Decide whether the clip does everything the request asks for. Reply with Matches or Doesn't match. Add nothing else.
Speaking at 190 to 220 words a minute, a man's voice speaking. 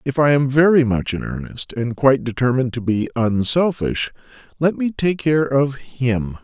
Doesn't match